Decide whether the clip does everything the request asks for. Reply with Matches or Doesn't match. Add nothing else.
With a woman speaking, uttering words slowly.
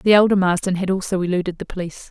Doesn't match